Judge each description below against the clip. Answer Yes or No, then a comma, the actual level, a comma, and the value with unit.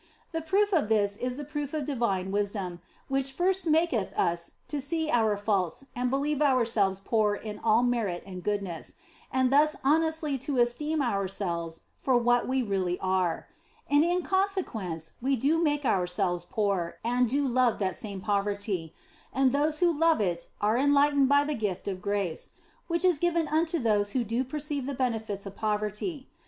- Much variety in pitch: Yes, wide, 6.5 semitones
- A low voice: No, high, 245 Hz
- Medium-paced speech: Yes, average, 170 wpm